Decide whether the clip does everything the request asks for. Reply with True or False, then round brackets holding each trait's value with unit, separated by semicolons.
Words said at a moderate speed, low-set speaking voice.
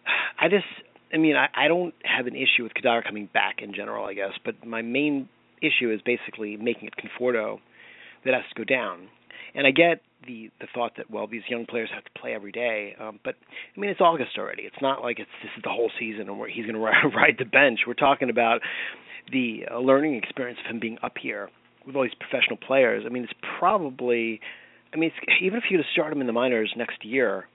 False (235 wpm; 120 Hz)